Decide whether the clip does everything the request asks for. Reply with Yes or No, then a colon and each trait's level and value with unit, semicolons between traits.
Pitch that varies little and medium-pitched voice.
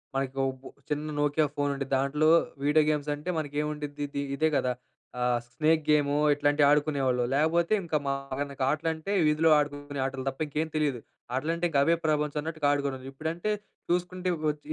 Yes: narrow, 1.9 semitones; medium, 145 Hz